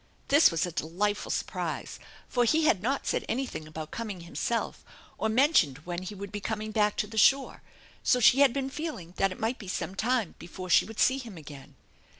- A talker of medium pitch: No, high, 215 Hz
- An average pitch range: No, wide, 5.9 semitones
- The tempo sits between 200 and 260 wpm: Yes, fast, 205 wpm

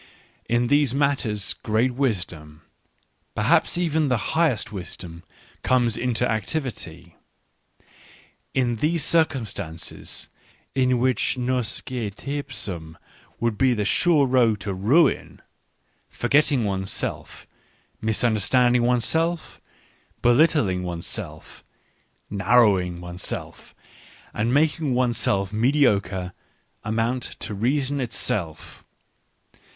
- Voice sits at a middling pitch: No, low, 120 Hz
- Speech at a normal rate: No, slow, 100 wpm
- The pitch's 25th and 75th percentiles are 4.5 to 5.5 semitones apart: Yes, average, 5.2 semitones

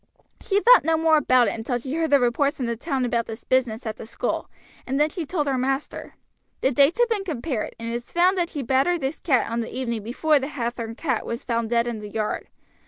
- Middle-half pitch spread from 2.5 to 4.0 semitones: No, average, 4.9 semitones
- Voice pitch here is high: Yes, very high, 260 Hz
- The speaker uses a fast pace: Yes, fast, 245 wpm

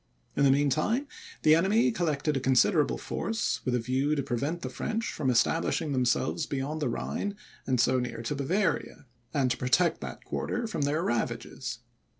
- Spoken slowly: No, average, 175 wpm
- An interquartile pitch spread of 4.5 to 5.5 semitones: Yes, average, 4.9 semitones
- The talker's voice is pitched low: No, medium, 145 Hz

